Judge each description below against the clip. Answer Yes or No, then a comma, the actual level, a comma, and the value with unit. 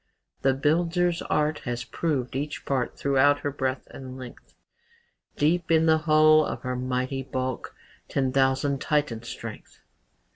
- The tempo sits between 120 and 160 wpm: Yes, average, 140 wpm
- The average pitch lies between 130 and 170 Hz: Yes, medium, 140 Hz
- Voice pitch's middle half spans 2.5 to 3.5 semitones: Yes, average, 3.0 semitones